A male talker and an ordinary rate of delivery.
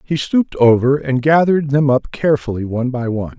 Yes: male; average, 195 wpm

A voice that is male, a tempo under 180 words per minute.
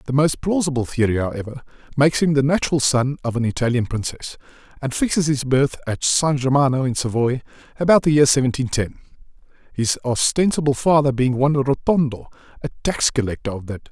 Yes: male; average, 170 wpm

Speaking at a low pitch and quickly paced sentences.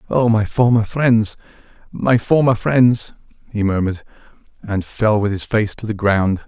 No: low, 110 Hz; average, 160 wpm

